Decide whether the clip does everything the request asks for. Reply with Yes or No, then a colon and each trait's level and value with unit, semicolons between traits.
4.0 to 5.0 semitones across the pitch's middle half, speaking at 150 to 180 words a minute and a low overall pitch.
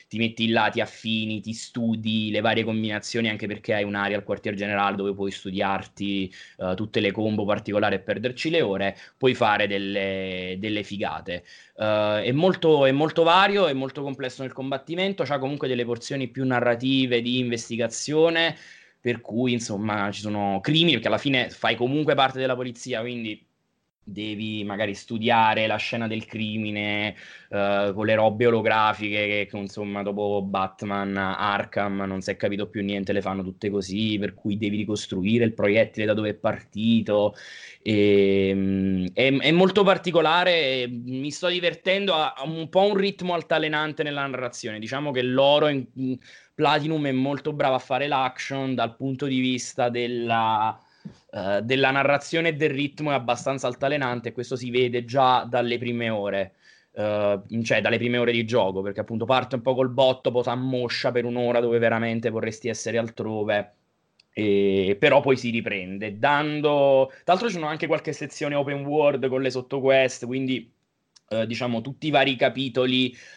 Yes: average, 4.3 semitones; average, 165 wpm; low, 120 Hz